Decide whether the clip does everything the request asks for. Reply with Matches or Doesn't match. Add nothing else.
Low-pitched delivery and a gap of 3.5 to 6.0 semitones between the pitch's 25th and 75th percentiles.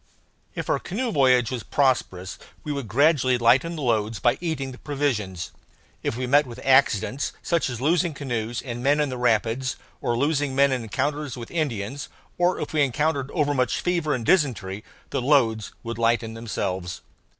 Matches